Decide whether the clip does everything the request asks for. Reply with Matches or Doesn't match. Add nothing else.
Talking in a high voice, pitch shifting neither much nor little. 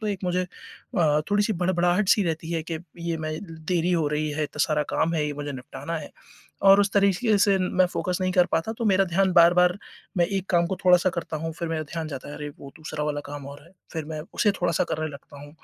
Doesn't match